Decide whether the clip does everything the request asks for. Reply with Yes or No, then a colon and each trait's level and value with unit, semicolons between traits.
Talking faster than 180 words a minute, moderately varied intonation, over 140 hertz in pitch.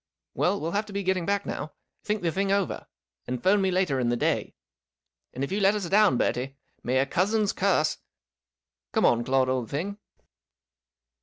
No: average, 190 wpm; wide, 6.9 semitones; medium, 185 Hz